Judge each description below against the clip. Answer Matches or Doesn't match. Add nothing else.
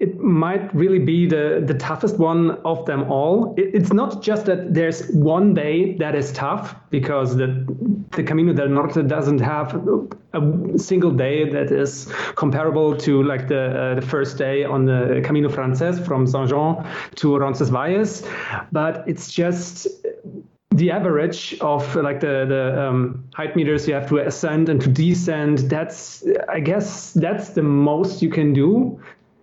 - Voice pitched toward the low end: Doesn't match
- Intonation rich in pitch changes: Doesn't match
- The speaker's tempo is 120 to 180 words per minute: Matches